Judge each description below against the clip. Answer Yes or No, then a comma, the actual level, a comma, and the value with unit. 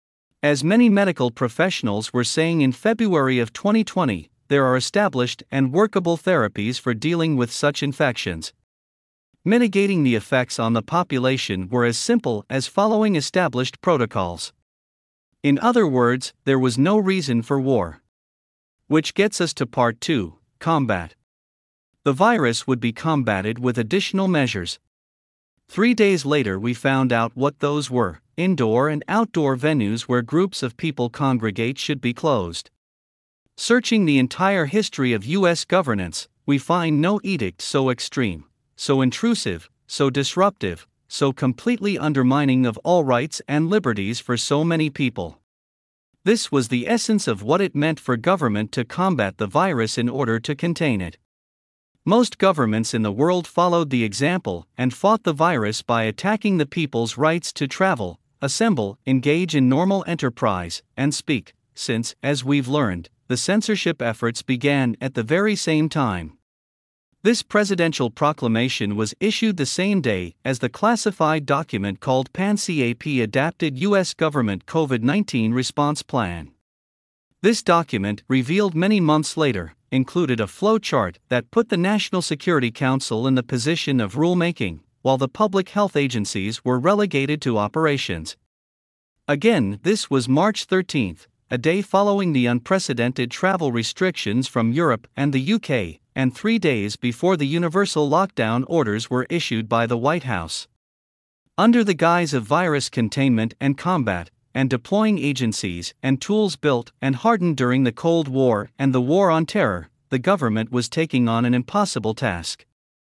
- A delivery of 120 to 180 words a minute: Yes, average, 150 wpm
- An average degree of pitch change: No, wide, 6.7 semitones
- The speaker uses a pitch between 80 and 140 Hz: Yes, low, 135 Hz